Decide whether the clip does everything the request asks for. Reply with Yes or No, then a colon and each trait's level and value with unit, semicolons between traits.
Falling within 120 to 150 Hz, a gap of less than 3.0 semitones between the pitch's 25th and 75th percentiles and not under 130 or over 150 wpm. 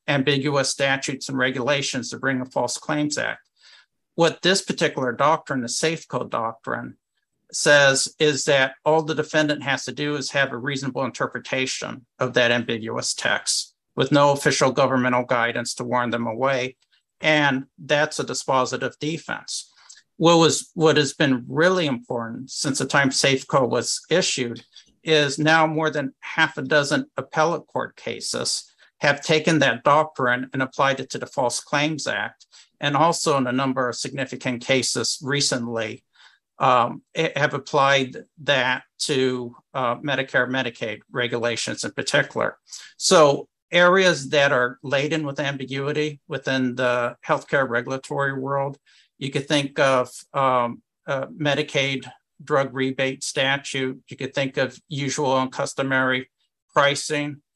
Yes: low, 135 Hz; narrow, 2.5 semitones; average, 140 wpm